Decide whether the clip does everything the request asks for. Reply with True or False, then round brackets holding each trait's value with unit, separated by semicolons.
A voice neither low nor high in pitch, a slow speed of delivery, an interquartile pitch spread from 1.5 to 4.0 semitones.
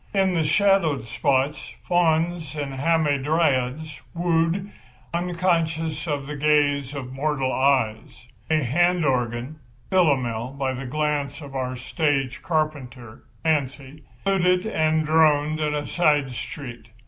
True (150 Hz; 110 wpm; 3.4 semitones)